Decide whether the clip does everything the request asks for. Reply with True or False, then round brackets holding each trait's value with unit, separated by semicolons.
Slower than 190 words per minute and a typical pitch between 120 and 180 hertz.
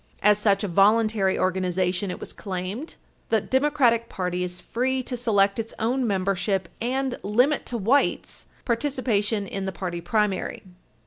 False (145 wpm; 210 Hz)